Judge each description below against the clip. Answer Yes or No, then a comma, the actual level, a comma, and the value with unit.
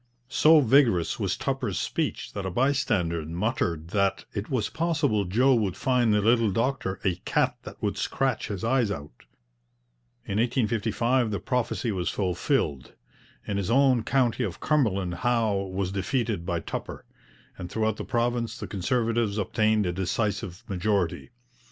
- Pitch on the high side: No, low, 110 Hz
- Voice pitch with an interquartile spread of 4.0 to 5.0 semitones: Yes, average, 4.3 semitones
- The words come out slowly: No, average, 150 wpm